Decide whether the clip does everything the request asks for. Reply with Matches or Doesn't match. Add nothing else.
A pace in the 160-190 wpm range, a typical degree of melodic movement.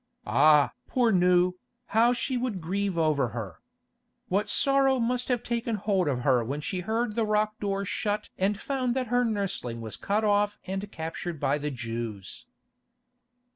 Doesn't match